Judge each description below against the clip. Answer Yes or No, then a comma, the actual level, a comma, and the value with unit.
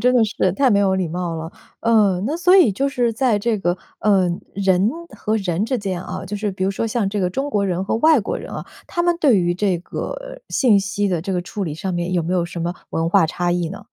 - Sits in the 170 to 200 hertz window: Yes, high, 195 Hz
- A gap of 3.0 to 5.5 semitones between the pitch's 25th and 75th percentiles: Yes, average, 4.3 semitones